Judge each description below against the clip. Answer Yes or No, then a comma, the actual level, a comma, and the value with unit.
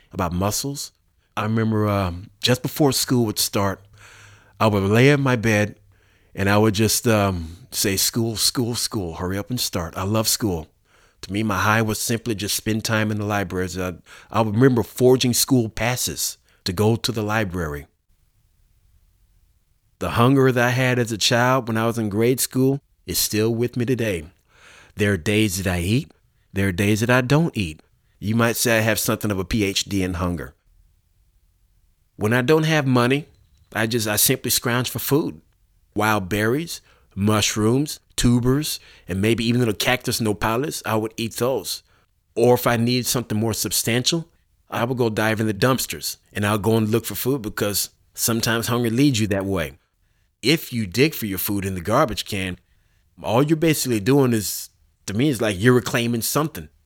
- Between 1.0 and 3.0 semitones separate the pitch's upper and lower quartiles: No, average, 3.9 semitones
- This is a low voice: Yes, low, 110 Hz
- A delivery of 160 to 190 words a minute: Yes, average, 185 wpm